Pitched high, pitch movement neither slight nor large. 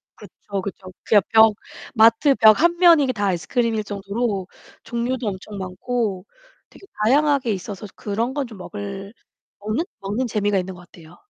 Yes: high, 215 Hz; average, 3.7 semitones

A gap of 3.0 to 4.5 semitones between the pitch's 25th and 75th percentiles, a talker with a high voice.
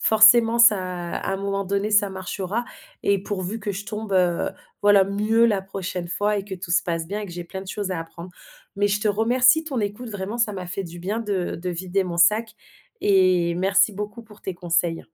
No: narrow, 2.6 semitones; high, 195 Hz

